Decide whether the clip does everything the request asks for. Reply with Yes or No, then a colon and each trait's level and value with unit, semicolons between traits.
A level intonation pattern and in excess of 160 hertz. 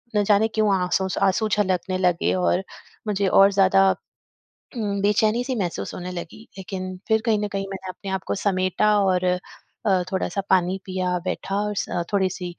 Yes: narrow, 1.9 semitones; high, 190 Hz